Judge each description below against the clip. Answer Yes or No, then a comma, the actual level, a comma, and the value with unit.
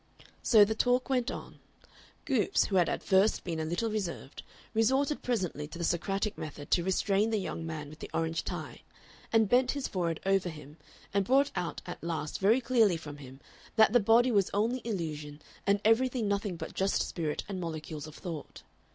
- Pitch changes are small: No, wide, 5.6 semitones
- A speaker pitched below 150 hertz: No, high, 195 Hz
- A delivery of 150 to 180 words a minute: No, average, 190 wpm